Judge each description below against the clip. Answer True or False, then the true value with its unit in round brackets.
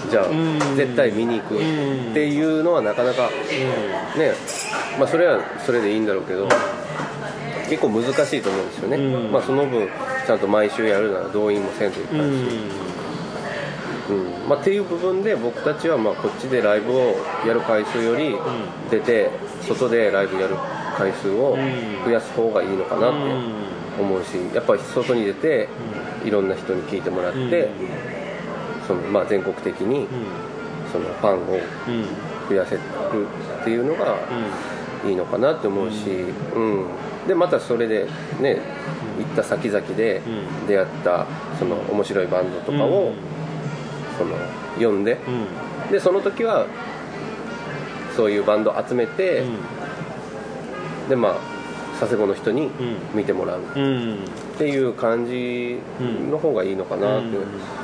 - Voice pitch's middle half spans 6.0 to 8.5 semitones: True (6.3 semitones)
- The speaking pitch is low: True (125 Hz)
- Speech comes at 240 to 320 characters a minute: True (270 characters per minute)